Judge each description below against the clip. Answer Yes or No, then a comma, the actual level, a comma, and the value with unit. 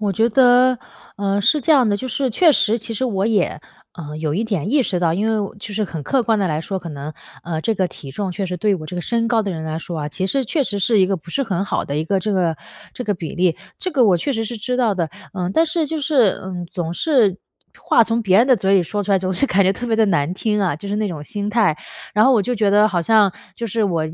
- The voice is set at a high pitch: Yes, high, 200 Hz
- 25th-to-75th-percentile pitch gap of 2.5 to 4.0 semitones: No, average, 4.4 semitones